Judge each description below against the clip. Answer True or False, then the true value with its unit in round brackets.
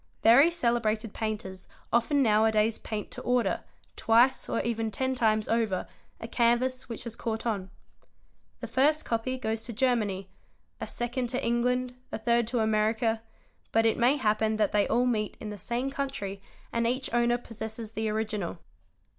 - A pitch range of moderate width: False (2.1 semitones)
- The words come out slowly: False (170 wpm)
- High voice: True (230 Hz)